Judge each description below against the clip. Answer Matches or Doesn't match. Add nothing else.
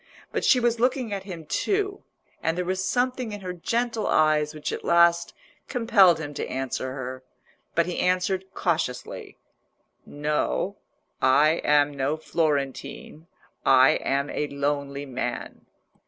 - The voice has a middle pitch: Matches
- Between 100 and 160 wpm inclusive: Matches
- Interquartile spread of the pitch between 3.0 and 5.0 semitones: Doesn't match